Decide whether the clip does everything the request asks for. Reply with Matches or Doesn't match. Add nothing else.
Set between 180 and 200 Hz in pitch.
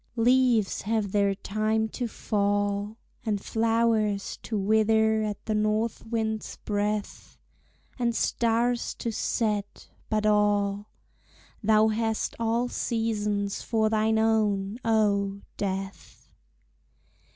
Doesn't match